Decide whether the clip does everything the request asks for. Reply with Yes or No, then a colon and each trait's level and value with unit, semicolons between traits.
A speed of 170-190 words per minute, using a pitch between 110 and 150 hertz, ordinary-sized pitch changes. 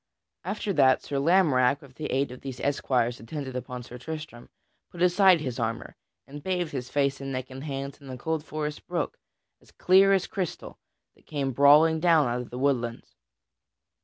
Yes: average, 185 wpm; medium, 140 Hz; average, 3.9 semitones